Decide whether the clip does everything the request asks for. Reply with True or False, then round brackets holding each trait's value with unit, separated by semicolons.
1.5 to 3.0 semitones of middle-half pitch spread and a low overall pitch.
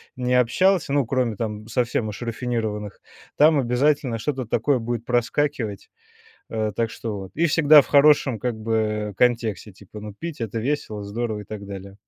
False (3.5 semitones; 115 Hz)